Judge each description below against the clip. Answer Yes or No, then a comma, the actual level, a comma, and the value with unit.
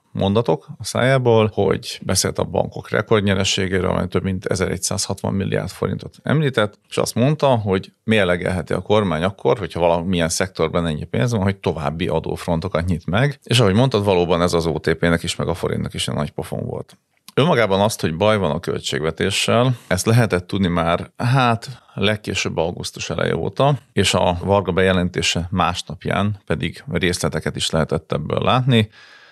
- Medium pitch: No, very low, 95 Hz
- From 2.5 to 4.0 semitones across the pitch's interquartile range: No, average, 4.4 semitones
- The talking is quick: Yes, fast, 160 wpm